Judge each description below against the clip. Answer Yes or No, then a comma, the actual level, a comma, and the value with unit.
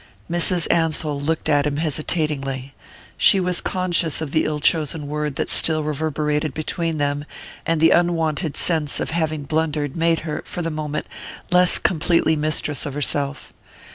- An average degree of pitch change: No, narrow, 1.9 semitones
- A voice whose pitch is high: No, medium, 155 Hz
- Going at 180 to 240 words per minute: No, average, 155 wpm